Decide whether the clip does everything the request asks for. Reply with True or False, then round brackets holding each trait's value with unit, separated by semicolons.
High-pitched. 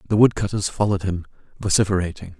False (95 Hz)